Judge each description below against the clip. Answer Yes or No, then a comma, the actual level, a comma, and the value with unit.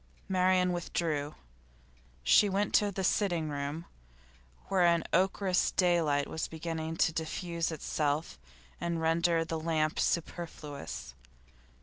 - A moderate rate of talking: No, slow, 115 wpm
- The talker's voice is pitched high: No, medium, 165 Hz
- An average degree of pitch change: No, narrow, 2.3 semitones